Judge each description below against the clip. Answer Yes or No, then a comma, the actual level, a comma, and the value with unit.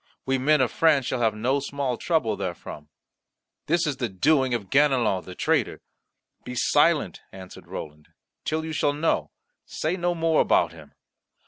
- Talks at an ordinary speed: Yes, average, 160 wpm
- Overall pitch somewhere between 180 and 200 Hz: No, low, 135 Hz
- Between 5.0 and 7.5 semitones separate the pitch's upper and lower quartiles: Yes, wide, 5.6 semitones